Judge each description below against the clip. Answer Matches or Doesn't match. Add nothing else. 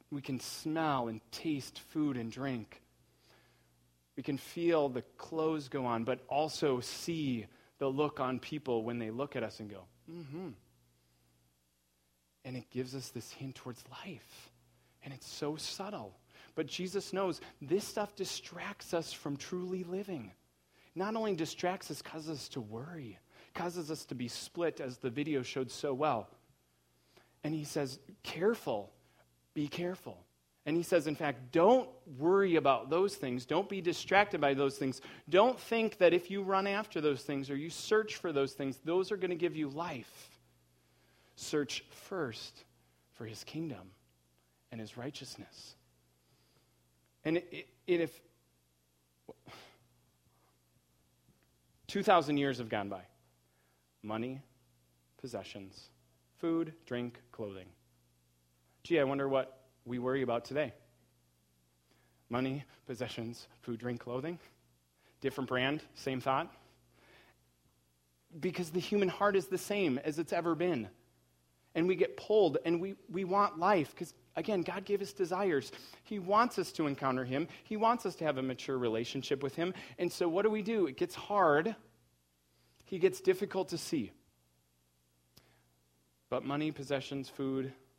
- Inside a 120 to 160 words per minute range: Matches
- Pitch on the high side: Doesn't match